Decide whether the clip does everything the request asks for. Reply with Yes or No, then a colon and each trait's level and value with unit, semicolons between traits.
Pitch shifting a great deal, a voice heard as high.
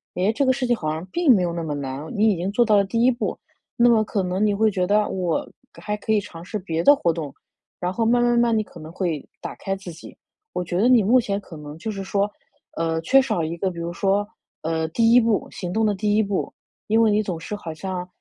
No: average, 4.4 semitones; high, 200 Hz